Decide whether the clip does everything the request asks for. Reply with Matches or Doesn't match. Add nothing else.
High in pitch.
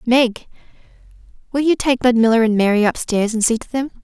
Matches